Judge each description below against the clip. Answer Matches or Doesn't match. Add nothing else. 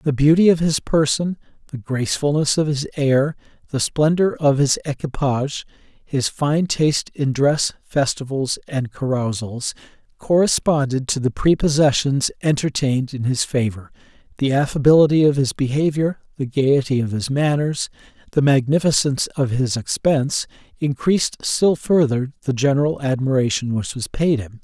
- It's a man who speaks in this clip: Matches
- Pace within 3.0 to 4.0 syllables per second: Doesn't match